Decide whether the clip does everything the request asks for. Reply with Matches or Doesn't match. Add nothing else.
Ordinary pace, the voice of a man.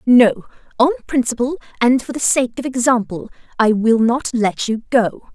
Doesn't match